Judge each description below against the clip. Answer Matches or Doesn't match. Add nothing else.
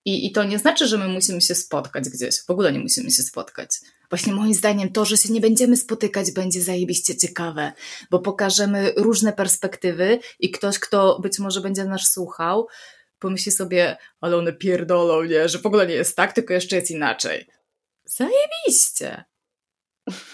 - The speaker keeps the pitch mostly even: Doesn't match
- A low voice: Doesn't match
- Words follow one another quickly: Matches